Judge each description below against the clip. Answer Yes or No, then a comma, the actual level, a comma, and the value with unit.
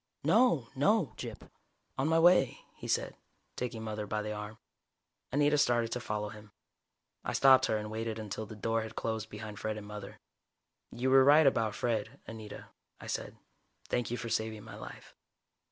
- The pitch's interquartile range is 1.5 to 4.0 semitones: Yes, average, 3.5 semitones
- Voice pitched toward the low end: Yes, low, 110 Hz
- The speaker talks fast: No, average, 175 wpm